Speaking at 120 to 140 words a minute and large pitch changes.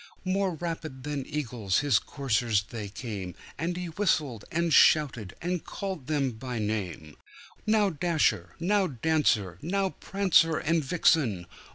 Yes: slow, 135 wpm; wide, 7.6 semitones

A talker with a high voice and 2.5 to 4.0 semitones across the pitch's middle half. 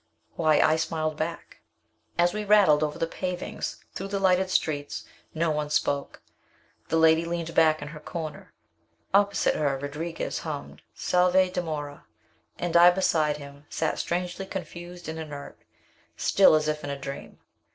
No: medium, 160 Hz; average, 2.8 semitones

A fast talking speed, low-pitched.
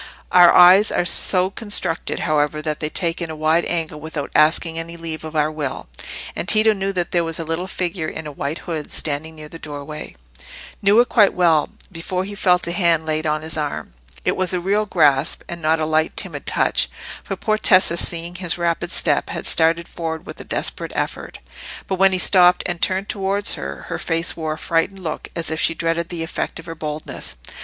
No: fast, 210 wpm; medium, 165 Hz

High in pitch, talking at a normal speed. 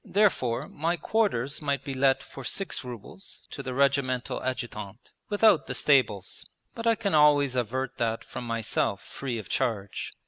No: low, 135 Hz; average, 160 wpm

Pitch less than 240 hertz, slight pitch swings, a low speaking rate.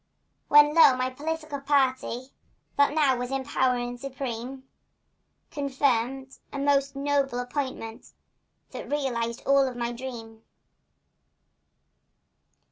No: very high, 265 Hz; narrow, 2.3 semitones; slow, 110 wpm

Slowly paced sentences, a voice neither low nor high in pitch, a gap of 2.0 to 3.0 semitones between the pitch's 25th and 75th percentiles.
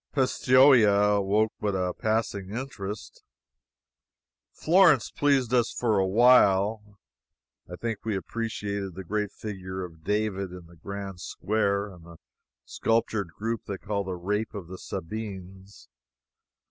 No: slow, 130 wpm; low, 100 Hz; average, 2.7 semitones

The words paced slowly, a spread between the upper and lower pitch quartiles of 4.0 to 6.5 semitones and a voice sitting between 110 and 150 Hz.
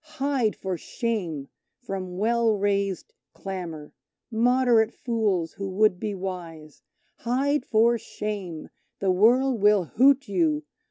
No: slow, 115 wpm; average, 4.4 semitones; high, 205 Hz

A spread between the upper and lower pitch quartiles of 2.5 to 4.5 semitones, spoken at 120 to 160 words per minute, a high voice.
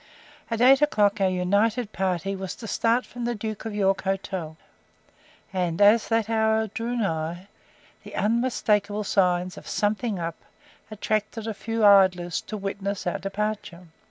Yes: average, 2.9 semitones; average, 150 wpm; high, 205 Hz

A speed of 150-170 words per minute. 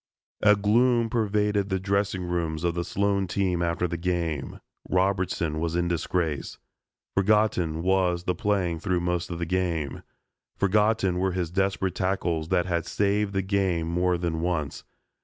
Yes: average, 155 wpm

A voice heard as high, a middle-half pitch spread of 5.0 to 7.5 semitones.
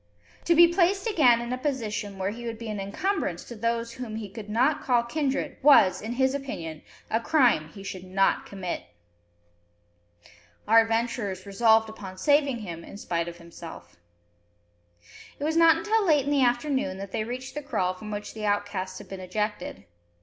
Yes: high, 225 Hz; wide, 5.6 semitones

